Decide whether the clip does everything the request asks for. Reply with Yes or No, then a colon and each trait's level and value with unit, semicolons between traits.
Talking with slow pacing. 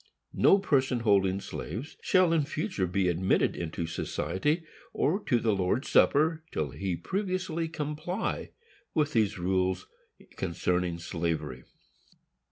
Yes: slow, 120 wpm